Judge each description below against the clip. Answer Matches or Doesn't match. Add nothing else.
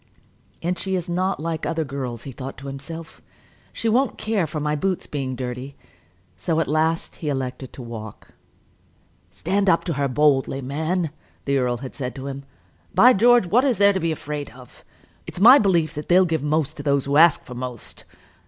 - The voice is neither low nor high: Matches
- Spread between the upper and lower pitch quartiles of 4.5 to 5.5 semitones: Matches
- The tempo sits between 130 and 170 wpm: Doesn't match